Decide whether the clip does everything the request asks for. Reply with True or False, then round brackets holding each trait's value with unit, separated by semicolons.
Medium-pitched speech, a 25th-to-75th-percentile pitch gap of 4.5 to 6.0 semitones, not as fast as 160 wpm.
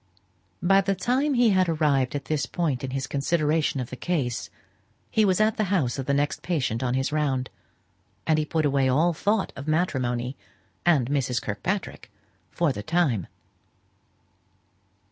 False (150 Hz; 5.1 semitones; 165 wpm)